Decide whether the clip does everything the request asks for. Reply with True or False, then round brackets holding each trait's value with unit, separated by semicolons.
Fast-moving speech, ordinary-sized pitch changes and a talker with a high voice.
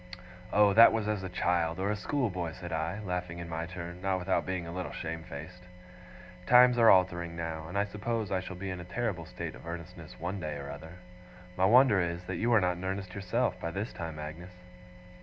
False (220 wpm; 3.0 semitones; 90 Hz)